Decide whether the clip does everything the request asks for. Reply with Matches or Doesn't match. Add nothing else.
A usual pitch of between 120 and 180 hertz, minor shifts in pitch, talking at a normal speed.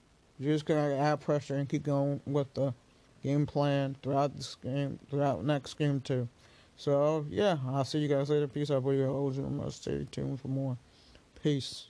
Matches